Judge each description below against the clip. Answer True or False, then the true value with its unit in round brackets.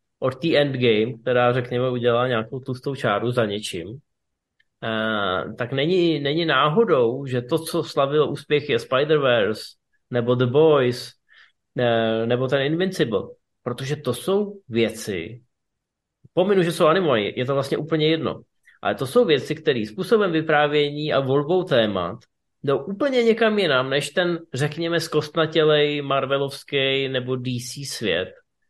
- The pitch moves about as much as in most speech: True (4.6 semitones)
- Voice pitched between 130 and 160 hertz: True (140 Hz)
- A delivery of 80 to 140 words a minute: True (135 wpm)